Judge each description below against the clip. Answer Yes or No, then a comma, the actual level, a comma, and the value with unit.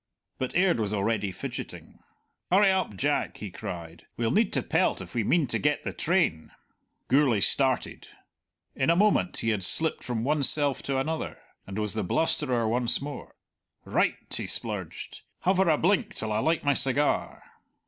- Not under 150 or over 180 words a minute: Yes, average, 170 wpm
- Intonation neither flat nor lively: No, wide, 6.7 semitones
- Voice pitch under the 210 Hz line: Yes, low, 135 Hz